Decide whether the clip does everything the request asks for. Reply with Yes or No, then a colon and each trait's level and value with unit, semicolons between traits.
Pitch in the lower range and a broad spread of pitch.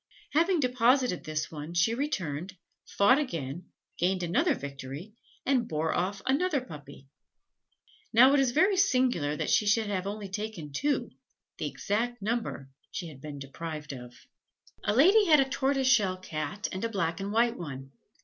No: high, 205 Hz; wide, 8.6 semitones